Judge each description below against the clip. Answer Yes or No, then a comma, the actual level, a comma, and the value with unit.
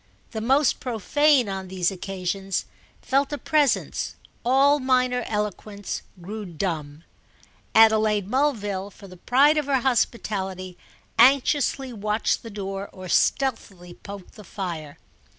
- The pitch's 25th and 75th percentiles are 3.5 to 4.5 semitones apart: No, average, 5.3 semitones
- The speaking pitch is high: Yes, high, 210 Hz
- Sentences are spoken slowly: Yes, slow, 120 wpm